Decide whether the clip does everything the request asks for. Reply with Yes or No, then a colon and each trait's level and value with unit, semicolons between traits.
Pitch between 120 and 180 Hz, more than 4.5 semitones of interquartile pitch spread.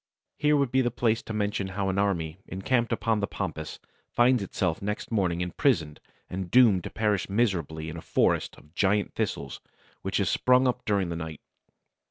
No: low, 100 Hz; average, 5.3 semitones